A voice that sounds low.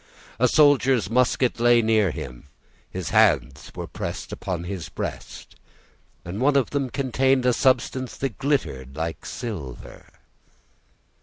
Yes: low, 115 Hz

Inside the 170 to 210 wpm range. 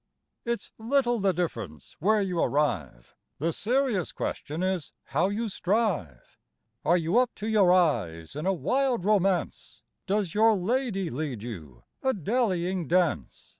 No: average, 140 wpm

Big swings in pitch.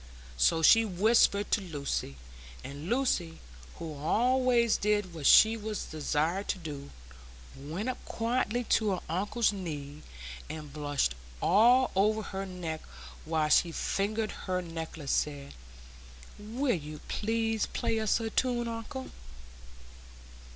Yes: wide, 6.2 semitones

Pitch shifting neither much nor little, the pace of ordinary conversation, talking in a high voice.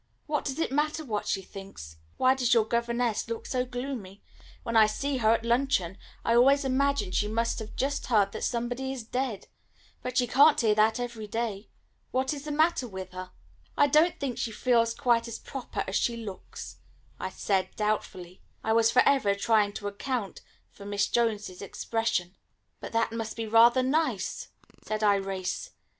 Yes: average, 3.8 semitones; average, 180 wpm; high, 230 Hz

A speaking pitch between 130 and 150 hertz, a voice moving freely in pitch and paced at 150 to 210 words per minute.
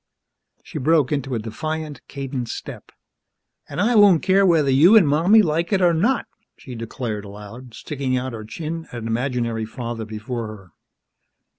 Yes: low, 135 Hz; wide, 6.2 semitones; average, 165 wpm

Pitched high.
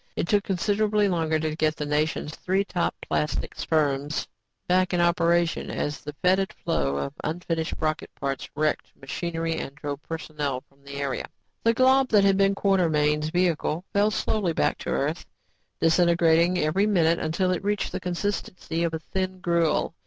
No: medium, 170 Hz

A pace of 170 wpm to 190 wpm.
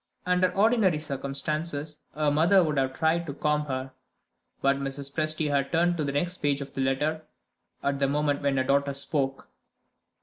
Yes: average, 175 wpm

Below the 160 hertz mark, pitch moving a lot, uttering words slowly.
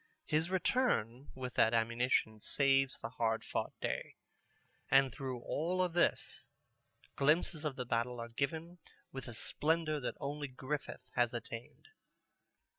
No: low, 135 Hz; average, 4.3 semitones; slow, 130 wpm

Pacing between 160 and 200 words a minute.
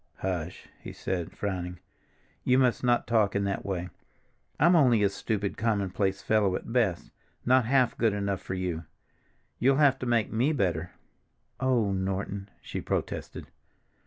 No: average, 150 wpm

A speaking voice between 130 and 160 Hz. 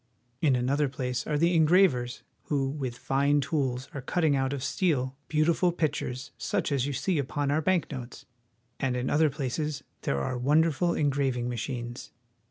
Yes: medium, 140 Hz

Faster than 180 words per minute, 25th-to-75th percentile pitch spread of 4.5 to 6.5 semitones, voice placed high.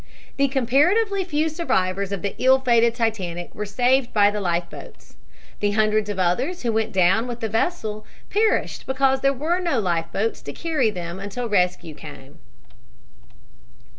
No: average, 165 wpm; wide, 5.6 semitones; high, 225 Hz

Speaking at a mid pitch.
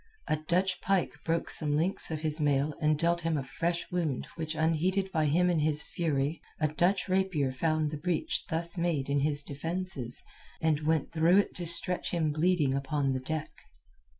Yes: medium, 160 Hz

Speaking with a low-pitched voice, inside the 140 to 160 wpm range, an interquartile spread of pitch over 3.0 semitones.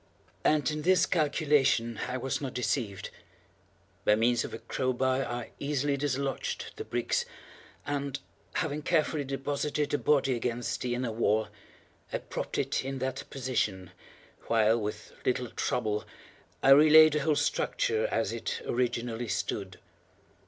Yes: low, 130 Hz; average, 145 wpm; average, 3.7 semitones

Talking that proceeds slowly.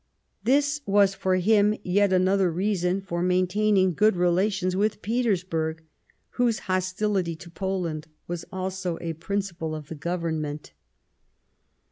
Yes: slow, 125 wpm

